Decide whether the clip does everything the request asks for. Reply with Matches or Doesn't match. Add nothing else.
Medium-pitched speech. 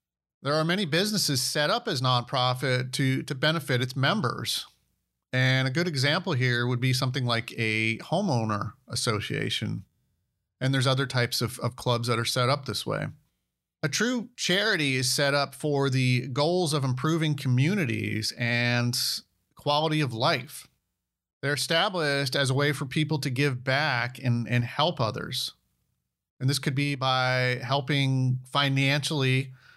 Doesn't match